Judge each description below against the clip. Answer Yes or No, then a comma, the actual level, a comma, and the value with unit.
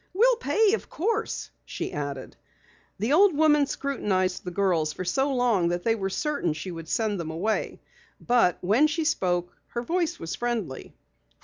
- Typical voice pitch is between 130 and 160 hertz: No, high, 220 Hz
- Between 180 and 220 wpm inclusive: No, average, 170 wpm